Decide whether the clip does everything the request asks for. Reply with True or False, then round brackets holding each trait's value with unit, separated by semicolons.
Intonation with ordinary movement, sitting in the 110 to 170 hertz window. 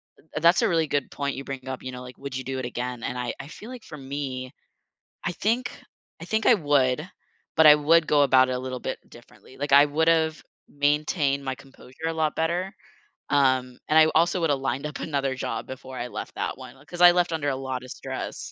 True (3.5 semitones; 140 Hz)